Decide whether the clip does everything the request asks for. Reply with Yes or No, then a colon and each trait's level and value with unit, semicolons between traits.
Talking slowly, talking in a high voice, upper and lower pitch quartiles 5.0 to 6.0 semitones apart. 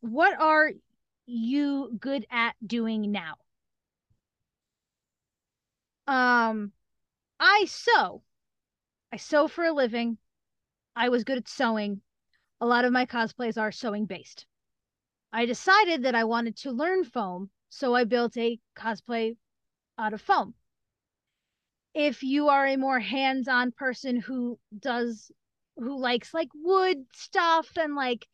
No: slow, 130 wpm; very high, 250 Hz; average, 3.8 semitones